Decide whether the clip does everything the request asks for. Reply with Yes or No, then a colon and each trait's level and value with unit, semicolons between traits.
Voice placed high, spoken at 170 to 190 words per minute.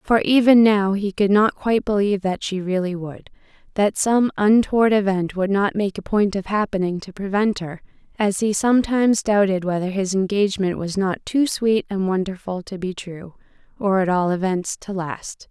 Yes: high, 200 Hz; average, 180 wpm